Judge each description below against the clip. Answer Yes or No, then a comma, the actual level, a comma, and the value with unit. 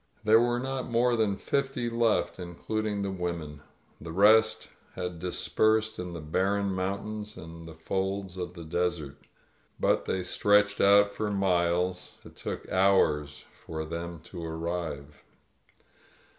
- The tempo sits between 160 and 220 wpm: No, average, 145 wpm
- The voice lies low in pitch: Yes, very low, 95 Hz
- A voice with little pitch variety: No, average, 3.8 semitones